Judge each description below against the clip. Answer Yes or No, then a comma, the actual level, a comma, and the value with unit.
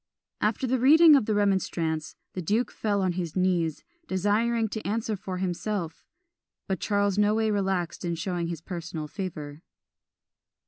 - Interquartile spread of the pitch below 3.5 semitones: No, average, 3.9 semitones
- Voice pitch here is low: No, high, 190 Hz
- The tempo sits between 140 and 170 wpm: Yes, average, 150 wpm